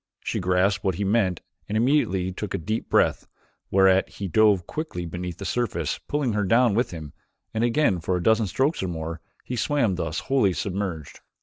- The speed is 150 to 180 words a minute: No, average, 190 wpm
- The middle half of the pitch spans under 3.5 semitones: No, average, 4.3 semitones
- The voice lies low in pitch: Yes, low, 100 Hz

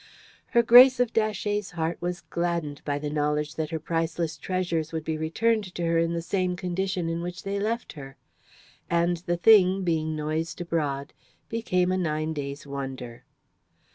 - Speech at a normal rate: Yes, average, 170 wpm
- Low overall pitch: No, medium, 170 Hz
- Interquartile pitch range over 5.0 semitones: No, average, 3.1 semitones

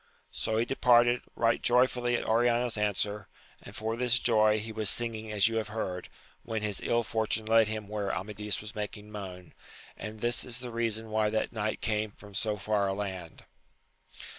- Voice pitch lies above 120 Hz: No, low, 110 Hz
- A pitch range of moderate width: No, narrow, 1.8 semitones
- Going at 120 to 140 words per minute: No, average, 185 wpm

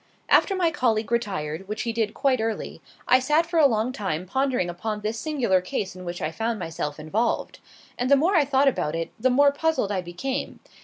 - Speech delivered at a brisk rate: Yes, fast, 210 wpm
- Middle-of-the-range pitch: No, high, 225 Hz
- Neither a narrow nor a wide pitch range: No, wide, 6.6 semitones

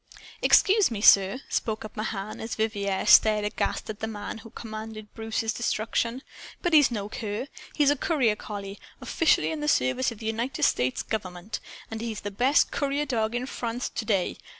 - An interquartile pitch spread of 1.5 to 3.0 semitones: Yes, average, 2.7 semitones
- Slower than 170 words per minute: No, average, 180 wpm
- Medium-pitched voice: No, high, 220 Hz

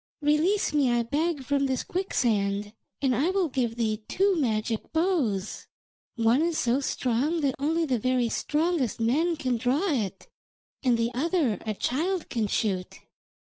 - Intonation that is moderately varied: No, wide, 5.7 semitones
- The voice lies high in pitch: Yes, very high, 260 Hz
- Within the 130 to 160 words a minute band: Yes, average, 155 wpm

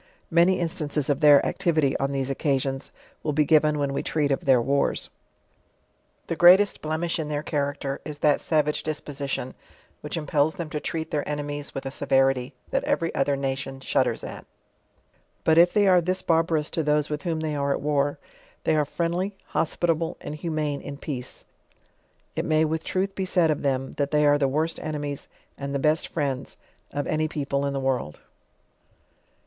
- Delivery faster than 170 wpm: Yes, average, 185 wpm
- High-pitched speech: No, medium, 150 Hz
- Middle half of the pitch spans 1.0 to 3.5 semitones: Yes, narrow, 2.4 semitones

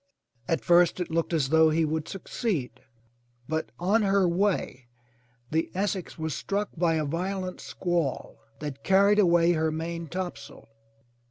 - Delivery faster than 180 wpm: No, average, 140 wpm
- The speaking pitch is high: No, medium, 170 Hz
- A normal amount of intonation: Yes, average, 3.0 semitones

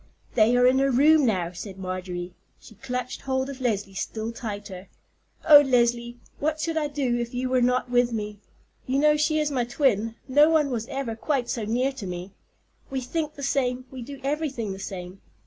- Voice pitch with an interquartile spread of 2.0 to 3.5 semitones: No, average, 4.1 semitones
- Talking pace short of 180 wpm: No, average, 200 wpm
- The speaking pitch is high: Yes, very high, 250 Hz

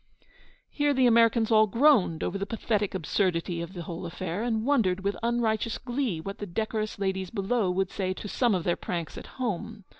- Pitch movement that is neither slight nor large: Yes, average, 3.9 semitones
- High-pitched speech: Yes, high, 205 Hz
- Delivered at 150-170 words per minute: No, average, 190 wpm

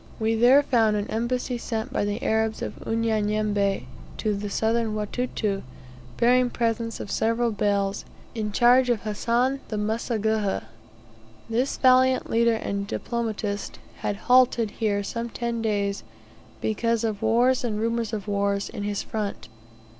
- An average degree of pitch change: No, narrow, 2.2 semitones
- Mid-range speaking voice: No, high, 220 Hz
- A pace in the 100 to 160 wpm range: Yes, average, 140 wpm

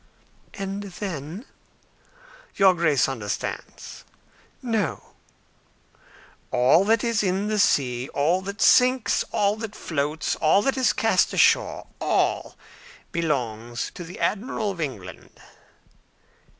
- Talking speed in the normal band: No, slow, 110 wpm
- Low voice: No, medium, 185 Hz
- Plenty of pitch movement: Yes, wide, 6.6 semitones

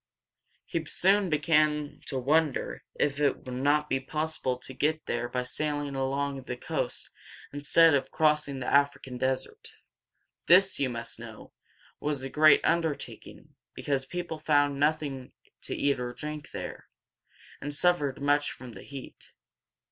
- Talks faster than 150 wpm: No, average, 145 wpm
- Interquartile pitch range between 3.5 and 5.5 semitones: No, narrow, 2.5 semitones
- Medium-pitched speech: Yes, medium, 145 Hz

